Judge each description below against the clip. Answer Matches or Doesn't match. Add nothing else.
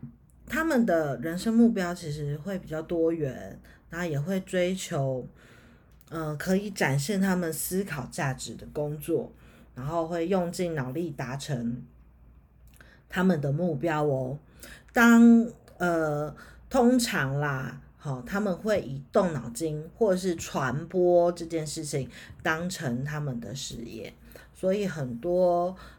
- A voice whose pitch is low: Doesn't match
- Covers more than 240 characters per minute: Doesn't match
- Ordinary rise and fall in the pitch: Matches